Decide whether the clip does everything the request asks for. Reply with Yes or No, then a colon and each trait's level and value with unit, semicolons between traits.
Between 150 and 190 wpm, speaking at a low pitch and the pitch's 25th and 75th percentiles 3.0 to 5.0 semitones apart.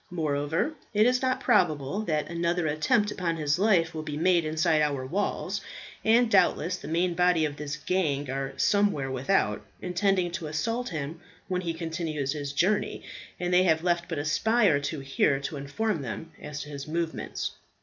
No: average, 180 wpm; medium, 165 Hz; average, 3.6 semitones